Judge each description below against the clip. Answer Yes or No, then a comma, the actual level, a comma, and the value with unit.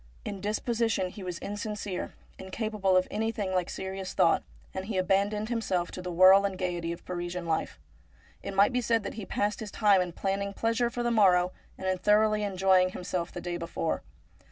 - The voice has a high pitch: Yes, high, 195 Hz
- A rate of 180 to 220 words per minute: Yes, average, 190 wpm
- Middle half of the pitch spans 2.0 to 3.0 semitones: Yes, narrow, 2.5 semitones